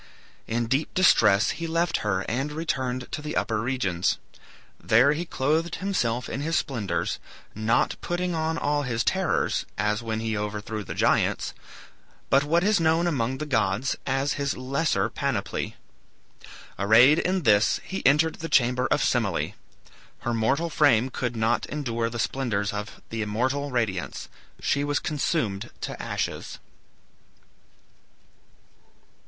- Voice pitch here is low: Yes, low, 130 Hz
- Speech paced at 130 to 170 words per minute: Yes, average, 140 wpm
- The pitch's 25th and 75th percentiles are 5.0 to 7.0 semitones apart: Yes, wide, 5.5 semitones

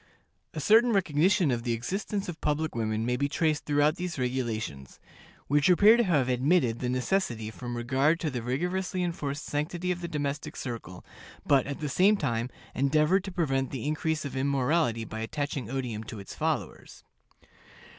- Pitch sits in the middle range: Yes, medium, 145 Hz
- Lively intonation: Yes, wide, 5.7 semitones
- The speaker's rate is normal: Yes, average, 170 wpm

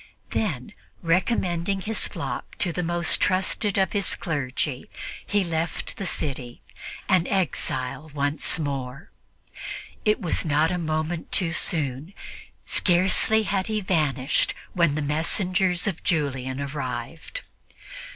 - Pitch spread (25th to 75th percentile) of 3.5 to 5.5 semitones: Yes, average, 4.7 semitones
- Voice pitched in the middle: Yes, medium, 165 Hz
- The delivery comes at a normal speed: No, slow, 120 wpm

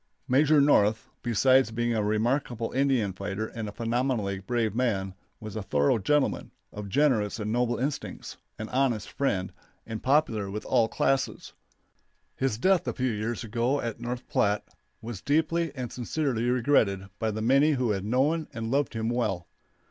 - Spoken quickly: No, average, 165 wpm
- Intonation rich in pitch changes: No, average, 3.8 semitones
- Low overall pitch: Yes, low, 120 Hz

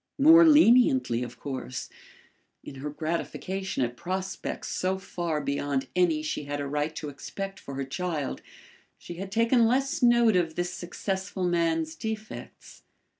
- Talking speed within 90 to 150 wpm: Yes, average, 145 wpm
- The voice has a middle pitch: Yes, medium, 175 Hz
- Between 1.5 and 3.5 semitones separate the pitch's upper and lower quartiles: No, average, 5.2 semitones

